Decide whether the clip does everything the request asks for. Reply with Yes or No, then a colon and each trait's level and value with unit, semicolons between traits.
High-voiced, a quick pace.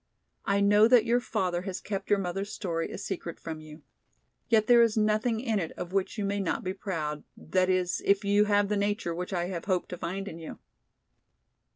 Yes: high, 195 Hz; fast, 215 wpm